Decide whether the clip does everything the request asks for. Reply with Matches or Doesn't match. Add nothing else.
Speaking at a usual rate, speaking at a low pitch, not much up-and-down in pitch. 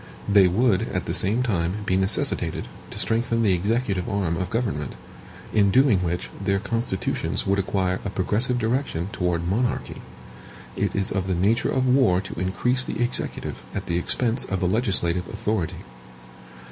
Doesn't match